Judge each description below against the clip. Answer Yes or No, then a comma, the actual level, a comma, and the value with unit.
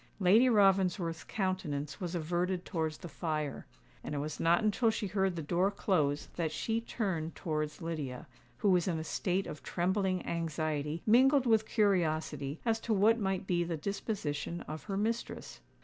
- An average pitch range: Yes, average, 4.2 semitones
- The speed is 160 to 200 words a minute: Yes, average, 165 wpm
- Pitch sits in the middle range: Yes, medium, 180 Hz